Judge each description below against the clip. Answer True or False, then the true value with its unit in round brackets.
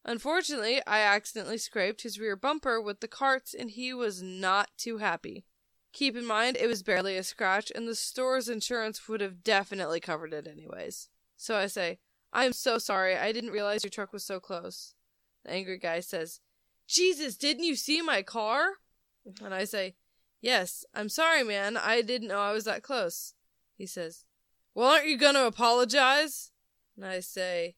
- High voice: True (220 Hz)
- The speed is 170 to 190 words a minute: True (180 wpm)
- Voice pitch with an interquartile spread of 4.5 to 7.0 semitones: True (4.8 semitones)